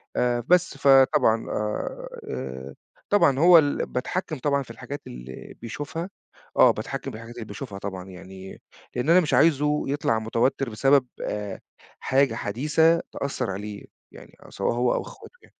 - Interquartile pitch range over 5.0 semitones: Yes, wide, 5.5 semitones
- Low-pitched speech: Yes, low, 125 Hz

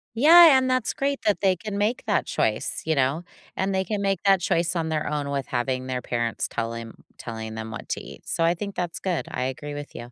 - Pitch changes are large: Yes, wide, 7.5 semitones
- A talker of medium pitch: Yes, medium, 165 Hz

